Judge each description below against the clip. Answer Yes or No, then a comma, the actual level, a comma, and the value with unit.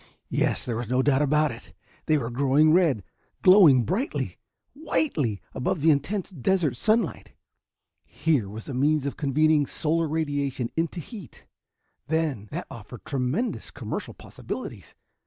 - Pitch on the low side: No, medium, 145 Hz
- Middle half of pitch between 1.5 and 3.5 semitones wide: No, average, 4.2 semitones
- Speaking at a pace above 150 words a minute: No, average, 140 wpm